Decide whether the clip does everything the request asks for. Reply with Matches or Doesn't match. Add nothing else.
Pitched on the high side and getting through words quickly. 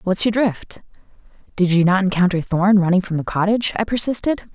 Doesn't match